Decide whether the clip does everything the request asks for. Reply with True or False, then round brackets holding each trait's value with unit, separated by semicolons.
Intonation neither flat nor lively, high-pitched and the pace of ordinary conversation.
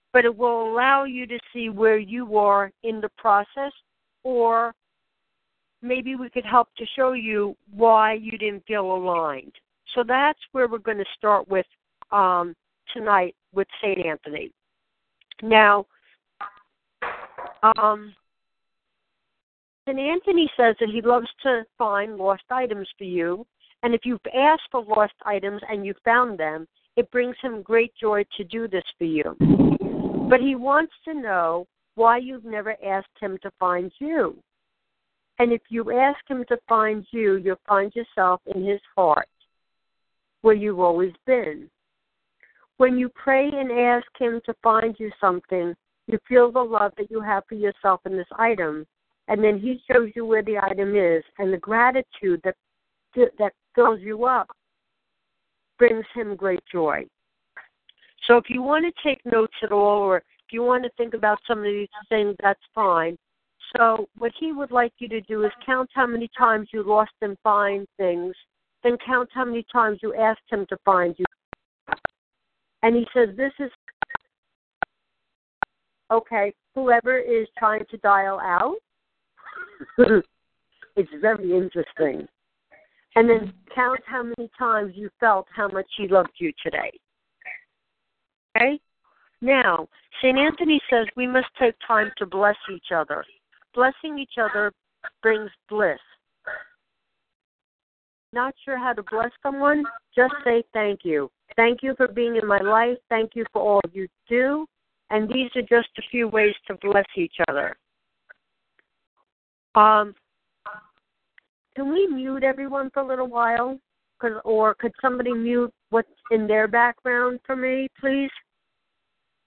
True (3.5 semitones; 225 Hz; 150 wpm)